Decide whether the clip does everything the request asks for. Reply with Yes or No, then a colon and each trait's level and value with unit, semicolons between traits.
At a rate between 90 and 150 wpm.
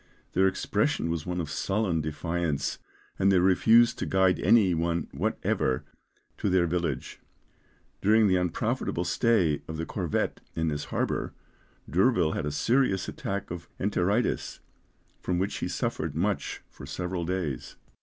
Yes: average, 145 wpm